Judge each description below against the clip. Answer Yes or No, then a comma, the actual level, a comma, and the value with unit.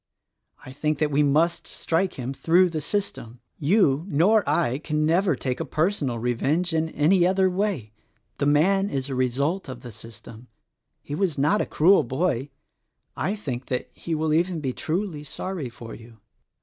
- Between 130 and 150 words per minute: No, average, 175 wpm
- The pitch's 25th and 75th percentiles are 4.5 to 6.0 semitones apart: Yes, wide, 5.5 semitones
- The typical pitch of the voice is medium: Yes, medium, 150 Hz